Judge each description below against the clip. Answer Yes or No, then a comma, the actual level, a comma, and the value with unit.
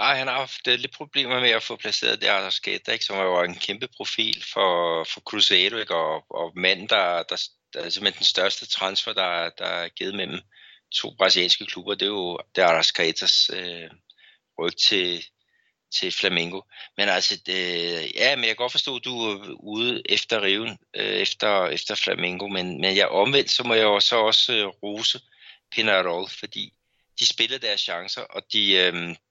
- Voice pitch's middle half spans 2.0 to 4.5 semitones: No, wide, 5.6 semitones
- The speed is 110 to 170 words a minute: No, average, 190 wpm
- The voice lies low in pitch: Yes, low, 100 Hz